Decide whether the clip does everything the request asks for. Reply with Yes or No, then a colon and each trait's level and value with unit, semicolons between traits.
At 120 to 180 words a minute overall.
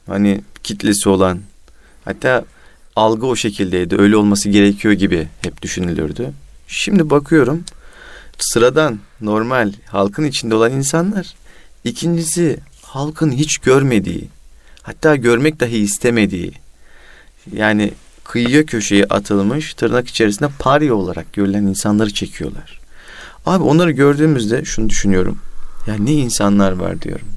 No: average, 110 wpm